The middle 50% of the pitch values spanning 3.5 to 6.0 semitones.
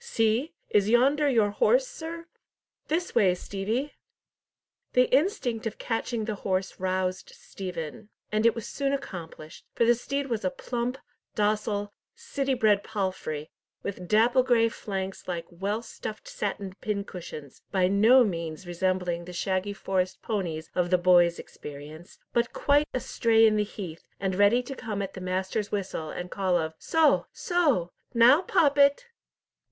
Yes: average, 5.1 semitones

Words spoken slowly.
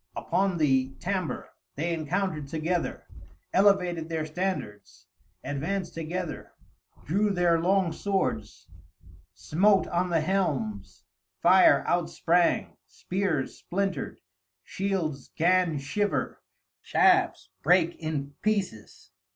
Yes: slow, 95 wpm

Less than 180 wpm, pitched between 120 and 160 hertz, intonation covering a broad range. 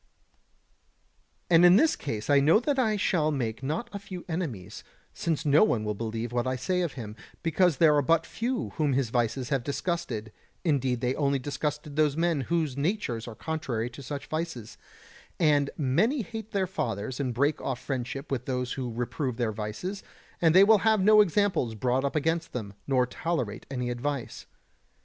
No: average, 185 wpm; medium, 140 Hz; wide, 5.7 semitones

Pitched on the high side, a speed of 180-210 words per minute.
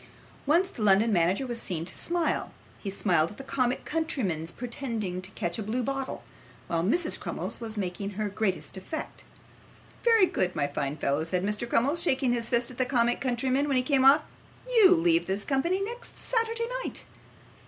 Yes: high, 240 Hz; average, 185 wpm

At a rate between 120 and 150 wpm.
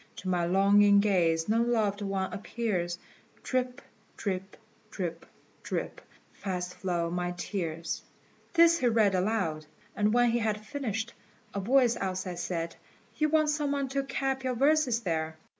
Yes: average, 145 wpm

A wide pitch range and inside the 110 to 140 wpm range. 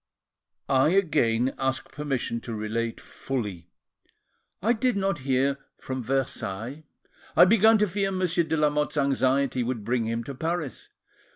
Yes: wide, 5.9 semitones; slow, 135 wpm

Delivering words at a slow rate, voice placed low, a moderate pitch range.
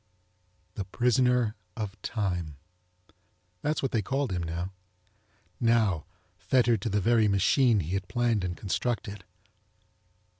Yes: slow, 120 wpm; low, 105 Hz; average, 4.4 semitones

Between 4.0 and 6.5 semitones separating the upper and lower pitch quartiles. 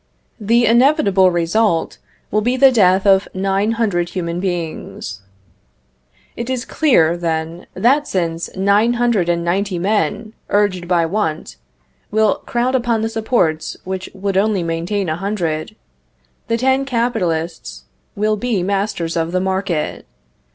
Yes: average, 4.6 semitones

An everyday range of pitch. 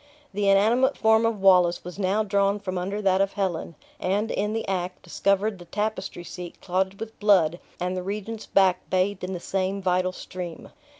No: narrow, 2.2 semitones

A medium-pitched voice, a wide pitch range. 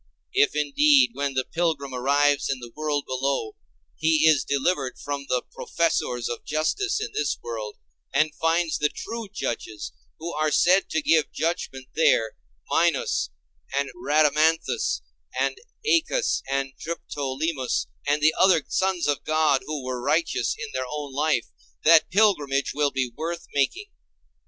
No: medium, 150 Hz; average, 3.3 semitones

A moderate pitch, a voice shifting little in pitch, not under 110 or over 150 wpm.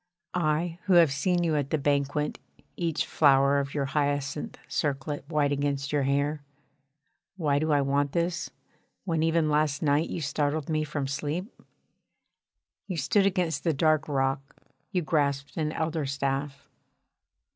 Yes: medium, 150 Hz; narrow, 2.2 semitones; average, 145 wpm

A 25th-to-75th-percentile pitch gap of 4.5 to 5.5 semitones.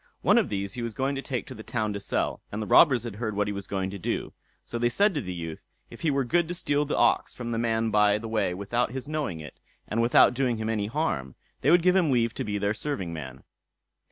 Yes: average, 5.0 semitones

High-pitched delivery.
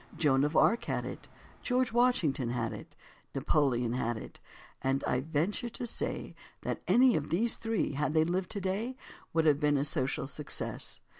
No: medium, 155 Hz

